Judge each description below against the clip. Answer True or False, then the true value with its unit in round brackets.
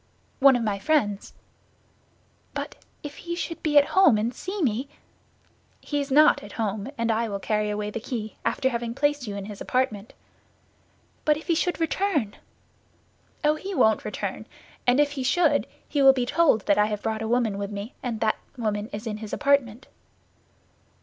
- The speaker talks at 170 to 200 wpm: True (185 wpm)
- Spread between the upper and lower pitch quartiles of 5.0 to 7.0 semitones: True (5.4 semitones)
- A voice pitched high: True (240 Hz)